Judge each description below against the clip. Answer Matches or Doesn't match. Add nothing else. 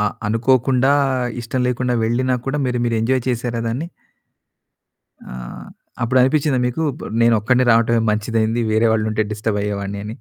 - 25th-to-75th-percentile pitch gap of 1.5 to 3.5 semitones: Matches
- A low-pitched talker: Matches